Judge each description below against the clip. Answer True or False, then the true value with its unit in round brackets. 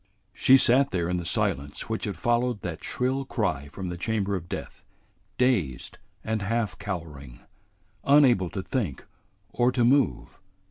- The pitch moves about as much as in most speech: False (6.1 semitones)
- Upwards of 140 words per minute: True (150 wpm)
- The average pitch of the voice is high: False (105 Hz)